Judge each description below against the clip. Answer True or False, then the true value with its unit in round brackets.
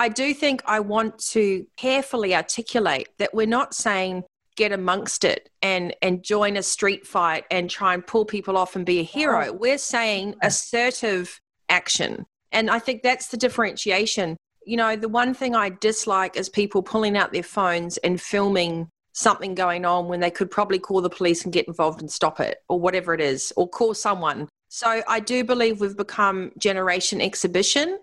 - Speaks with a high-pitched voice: True (200 Hz)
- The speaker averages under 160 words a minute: False (185 wpm)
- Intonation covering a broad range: False (3.9 semitones)